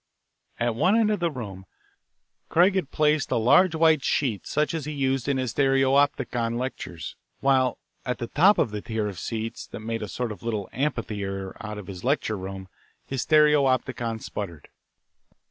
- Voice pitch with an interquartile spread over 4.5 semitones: Yes, average, 5.2 semitones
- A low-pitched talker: Yes, low, 125 Hz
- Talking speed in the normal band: Yes, average, 175 wpm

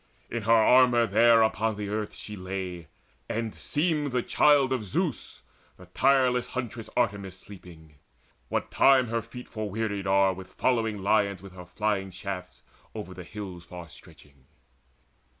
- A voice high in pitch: No, low, 105 Hz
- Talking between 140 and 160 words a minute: Yes, average, 150 wpm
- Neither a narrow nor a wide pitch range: Yes, average, 4.2 semitones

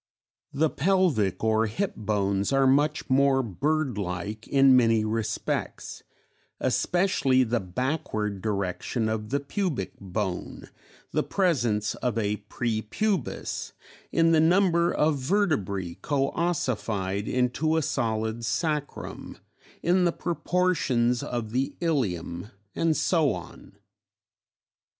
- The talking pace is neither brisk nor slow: No, slow, 110 wpm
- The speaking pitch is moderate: No, low, 125 Hz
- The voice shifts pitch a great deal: Yes, wide, 6.7 semitones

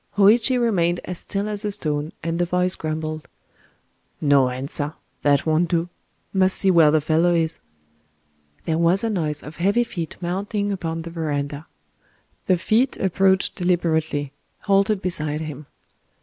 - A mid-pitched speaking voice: Yes, medium, 170 Hz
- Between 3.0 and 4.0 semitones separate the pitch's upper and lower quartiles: Yes, average, 3.7 semitones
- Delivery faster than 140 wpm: No, slow, 135 wpm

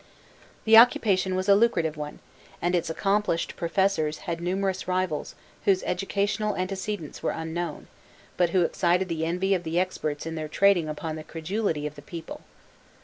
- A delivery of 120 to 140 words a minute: No, average, 160 wpm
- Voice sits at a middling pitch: Yes, medium, 180 Hz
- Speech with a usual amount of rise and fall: Yes, average, 3.2 semitones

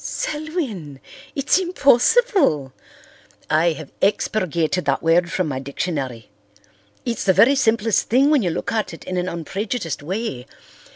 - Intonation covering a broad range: Yes, wide, 7.7 semitones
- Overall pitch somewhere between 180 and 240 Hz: Yes, medium, 185 Hz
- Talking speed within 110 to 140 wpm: Yes, slow, 135 wpm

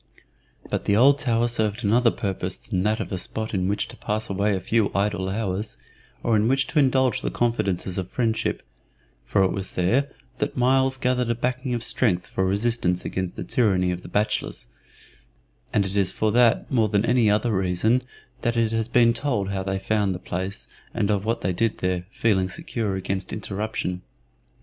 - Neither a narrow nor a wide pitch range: Yes, average, 3.7 semitones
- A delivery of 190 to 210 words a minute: Yes, average, 195 wpm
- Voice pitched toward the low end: Yes, low, 105 Hz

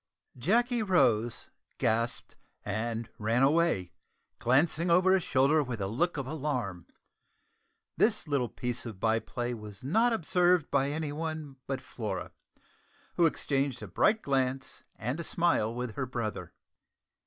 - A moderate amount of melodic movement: No, wide, 6.0 semitones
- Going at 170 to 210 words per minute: No, average, 140 wpm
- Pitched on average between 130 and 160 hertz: Yes, low, 135 Hz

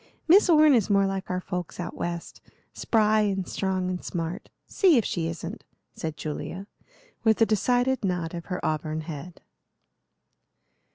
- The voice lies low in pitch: No, medium, 185 Hz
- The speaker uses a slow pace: No, average, 155 wpm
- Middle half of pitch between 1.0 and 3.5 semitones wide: No, average, 4.3 semitones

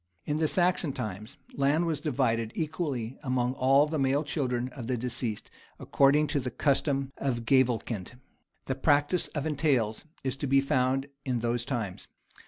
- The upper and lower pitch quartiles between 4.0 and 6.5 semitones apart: No, average, 3.2 semitones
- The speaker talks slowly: No, average, 160 wpm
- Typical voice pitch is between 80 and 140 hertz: Yes, low, 135 Hz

